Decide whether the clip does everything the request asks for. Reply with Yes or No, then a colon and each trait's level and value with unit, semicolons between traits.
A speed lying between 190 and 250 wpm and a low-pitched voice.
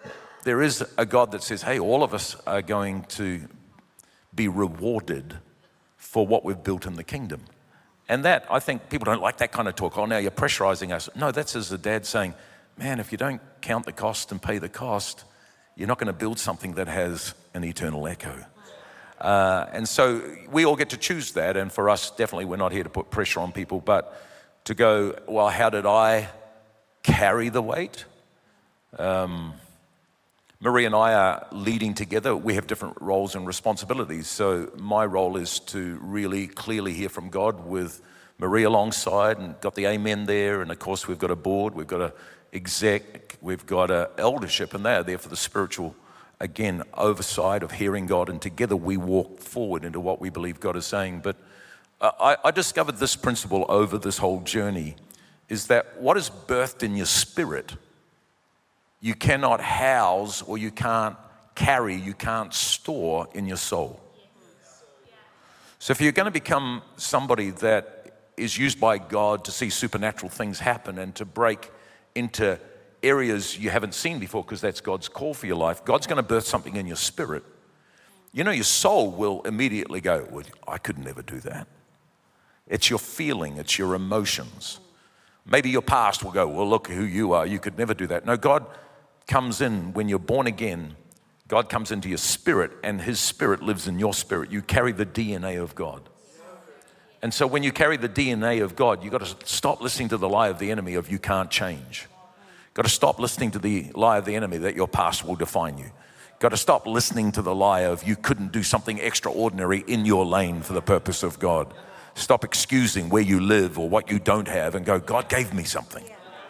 Yes: average, 195 wpm; low, 100 Hz